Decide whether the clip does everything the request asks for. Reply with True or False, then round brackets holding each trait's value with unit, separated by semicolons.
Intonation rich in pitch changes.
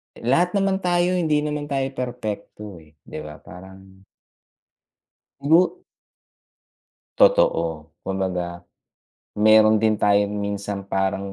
True (7.6 semitones)